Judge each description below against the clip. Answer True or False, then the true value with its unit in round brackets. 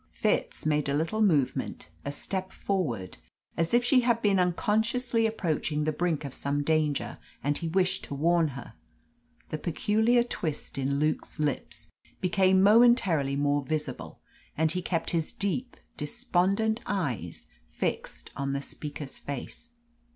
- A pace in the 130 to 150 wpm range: True (145 wpm)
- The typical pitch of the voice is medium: True (165 Hz)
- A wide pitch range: True (6.1 semitones)